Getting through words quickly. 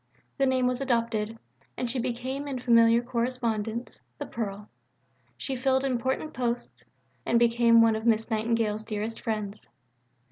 No: average, 140 wpm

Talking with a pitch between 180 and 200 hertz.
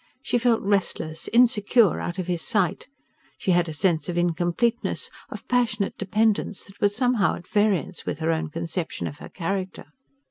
Yes: high, 190 Hz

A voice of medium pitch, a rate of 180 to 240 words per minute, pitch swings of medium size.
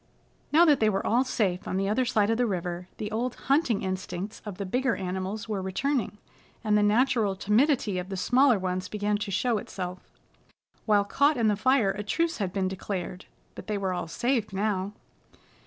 No: high, 210 Hz; average, 195 wpm; average, 4.0 semitones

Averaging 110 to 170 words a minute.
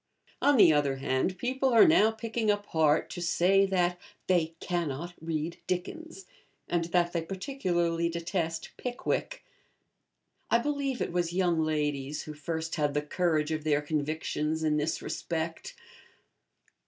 Yes: average, 140 wpm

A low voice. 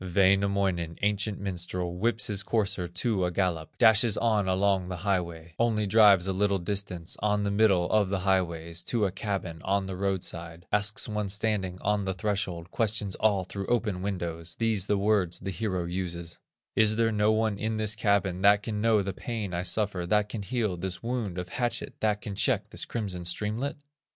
Yes: low, 100 Hz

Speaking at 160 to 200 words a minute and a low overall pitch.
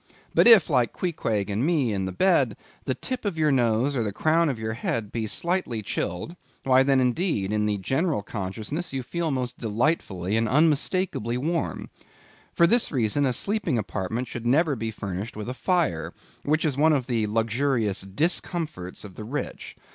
Yes: average, 180 wpm; low, 125 Hz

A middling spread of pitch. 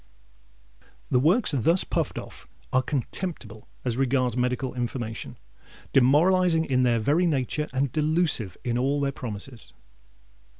Yes: average, 3.9 semitones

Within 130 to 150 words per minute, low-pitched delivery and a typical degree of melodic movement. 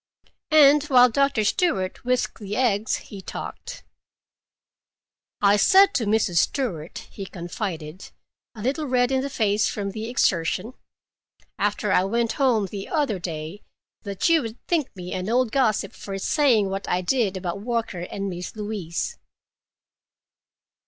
No: average, 145 wpm; high, 210 Hz; average, 4.9 semitones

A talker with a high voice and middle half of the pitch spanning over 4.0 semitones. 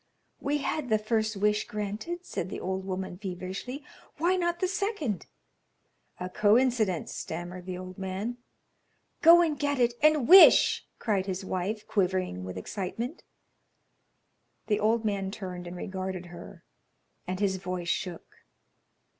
Yes: high, 200 Hz; average, 5.1 semitones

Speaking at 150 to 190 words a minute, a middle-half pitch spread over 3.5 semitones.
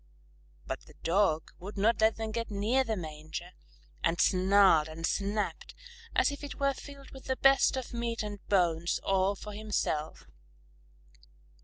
Yes: average, 155 wpm; average, 4.6 semitones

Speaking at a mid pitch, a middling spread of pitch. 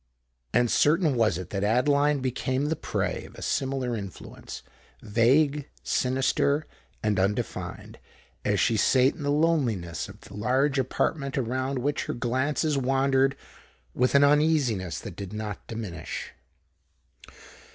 No: low, 130 Hz; average, 4.3 semitones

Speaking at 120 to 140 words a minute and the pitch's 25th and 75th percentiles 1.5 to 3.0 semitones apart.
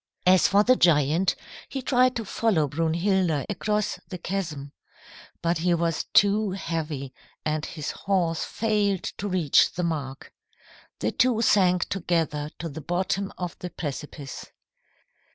No: slow, 135 wpm; average, 4.1 semitones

